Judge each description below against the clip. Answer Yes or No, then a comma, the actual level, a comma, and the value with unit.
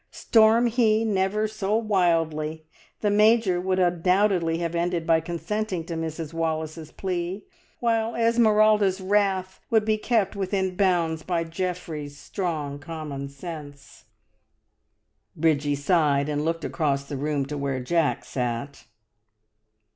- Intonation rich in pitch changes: No, average, 4.7 semitones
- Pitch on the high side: No, medium, 175 Hz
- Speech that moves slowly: Yes, slow, 125 wpm